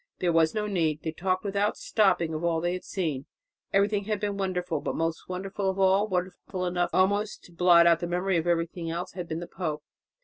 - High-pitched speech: No, medium, 180 Hz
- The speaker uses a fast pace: Yes, fast, 215 wpm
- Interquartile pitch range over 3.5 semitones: No, narrow, 2.6 semitones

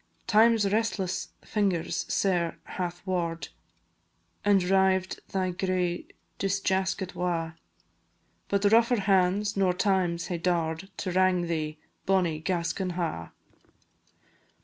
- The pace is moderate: No, slow, 105 wpm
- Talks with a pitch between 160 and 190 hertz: Yes, medium, 185 Hz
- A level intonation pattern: Yes, narrow, 2.1 semitones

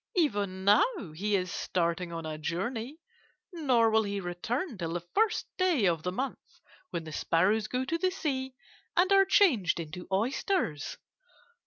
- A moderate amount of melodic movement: No, wide, 8.2 semitones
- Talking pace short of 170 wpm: Yes, average, 160 wpm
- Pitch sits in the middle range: No, high, 210 Hz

